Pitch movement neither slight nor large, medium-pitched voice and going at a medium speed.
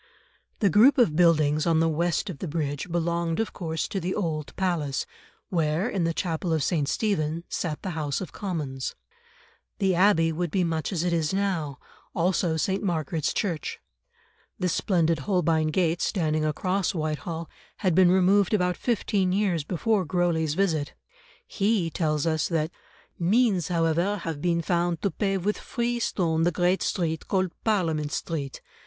Yes: average, 3.1 semitones; medium, 170 Hz; average, 160 wpm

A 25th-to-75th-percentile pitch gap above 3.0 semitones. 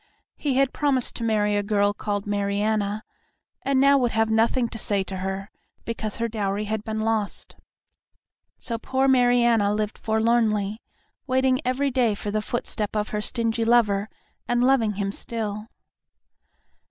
No: average, 2.7 semitones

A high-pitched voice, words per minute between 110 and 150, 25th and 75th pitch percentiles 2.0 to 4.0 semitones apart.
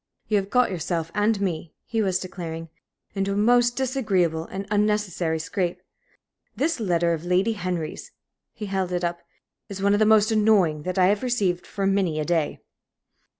No: high, 195 Hz; average, 175 wpm; average, 3.4 semitones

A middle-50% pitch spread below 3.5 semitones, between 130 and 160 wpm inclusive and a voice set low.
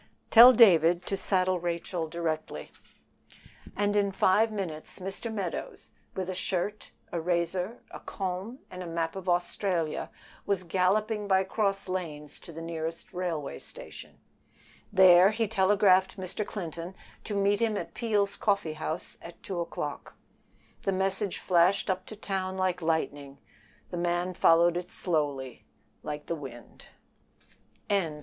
No: average, 2.8 semitones; average, 140 wpm; medium, 185 Hz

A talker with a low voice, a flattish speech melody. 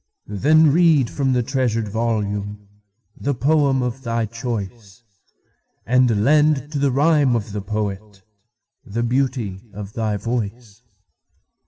No: low, 115 Hz; average, 4.4 semitones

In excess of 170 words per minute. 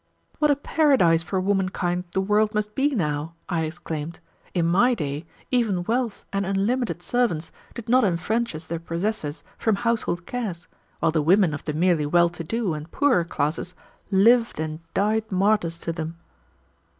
No: average, 160 wpm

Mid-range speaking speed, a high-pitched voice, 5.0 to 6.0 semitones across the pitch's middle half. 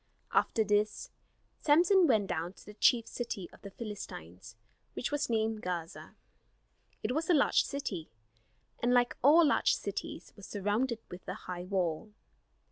Yes: average, 150 wpm; high, 215 Hz; average, 5.3 semitones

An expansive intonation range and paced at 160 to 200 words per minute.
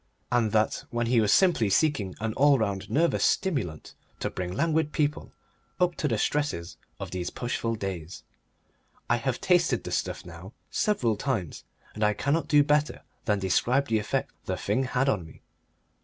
Yes: wide, 6.6 semitones; average, 170 wpm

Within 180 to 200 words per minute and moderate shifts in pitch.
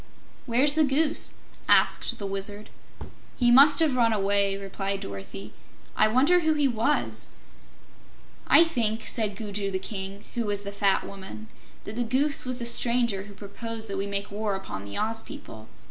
No: average, 170 wpm; average, 3.8 semitones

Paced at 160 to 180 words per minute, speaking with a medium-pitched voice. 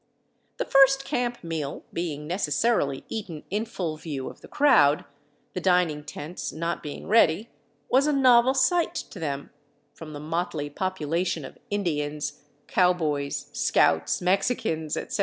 No: average, 140 wpm; medium, 170 Hz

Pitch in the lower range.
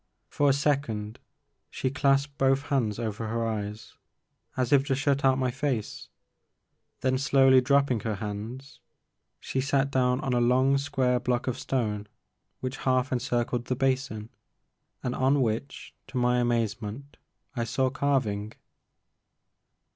Yes: low, 130 Hz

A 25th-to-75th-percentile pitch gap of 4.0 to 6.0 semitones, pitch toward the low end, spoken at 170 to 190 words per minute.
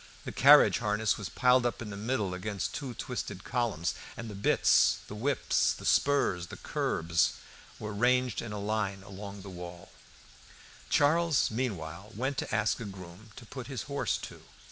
Yes: average, 4.3 semitones; low, 105 Hz; average, 175 wpm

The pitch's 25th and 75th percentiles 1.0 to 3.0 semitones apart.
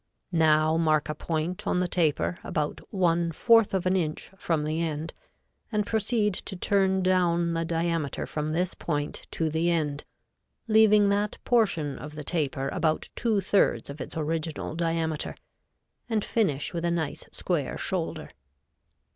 No: average, 3.5 semitones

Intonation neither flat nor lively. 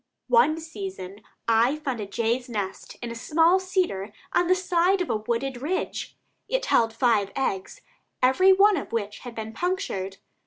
No: wide, 8.7 semitones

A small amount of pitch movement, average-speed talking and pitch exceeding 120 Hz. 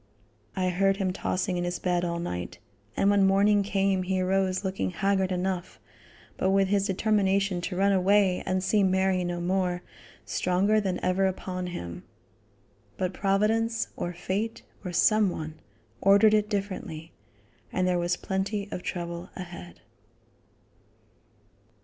Yes: narrow, 1.8 semitones; average, 145 wpm; high, 190 Hz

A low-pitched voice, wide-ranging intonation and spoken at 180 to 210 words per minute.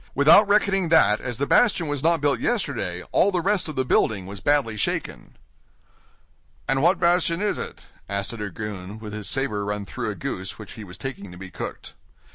Yes: low, 130 Hz; wide, 8.5 semitones; average, 200 wpm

